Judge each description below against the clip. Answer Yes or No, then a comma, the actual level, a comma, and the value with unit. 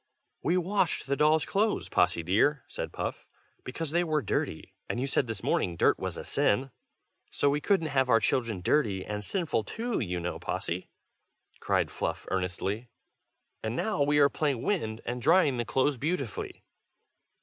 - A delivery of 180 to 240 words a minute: No, average, 170 wpm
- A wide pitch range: Yes, wide, 6.1 semitones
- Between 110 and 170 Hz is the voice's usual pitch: Yes, low, 135 Hz